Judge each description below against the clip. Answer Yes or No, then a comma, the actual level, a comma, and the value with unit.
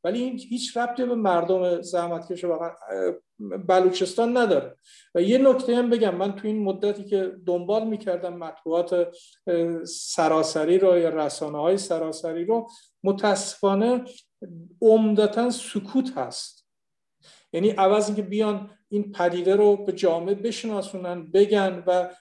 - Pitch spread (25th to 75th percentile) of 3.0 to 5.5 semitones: Yes, average, 3.6 semitones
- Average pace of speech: Yes, average, 125 wpm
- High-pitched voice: Yes, high, 195 Hz